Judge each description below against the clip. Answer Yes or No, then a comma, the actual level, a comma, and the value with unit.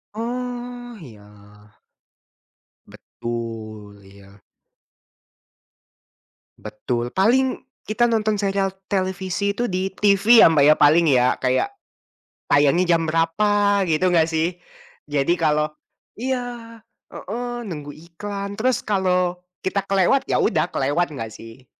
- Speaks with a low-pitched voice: No, medium, 180 Hz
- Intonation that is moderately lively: No, wide, 6.4 semitones